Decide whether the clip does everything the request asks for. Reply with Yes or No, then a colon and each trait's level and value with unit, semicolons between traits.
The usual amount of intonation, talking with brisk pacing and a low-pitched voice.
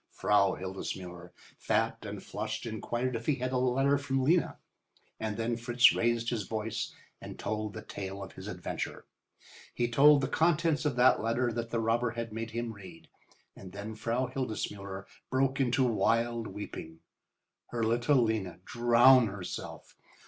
No: average, 3.0 semitones; average, 155 wpm; low, 115 Hz